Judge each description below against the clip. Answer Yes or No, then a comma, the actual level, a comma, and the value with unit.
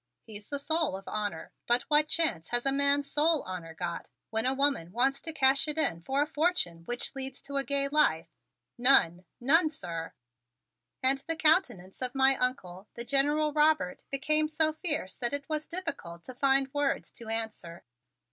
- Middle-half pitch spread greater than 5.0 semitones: Yes, wide, 5.5 semitones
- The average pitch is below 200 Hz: No, very high, 275 Hz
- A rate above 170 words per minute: Yes, average, 185 wpm